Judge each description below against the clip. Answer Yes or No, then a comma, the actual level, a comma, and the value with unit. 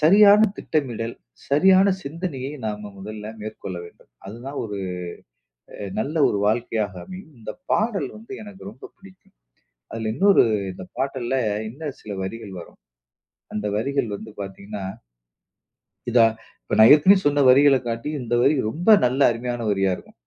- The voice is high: No, low, 125 Hz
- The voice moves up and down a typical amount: No, wide, 6.2 semitones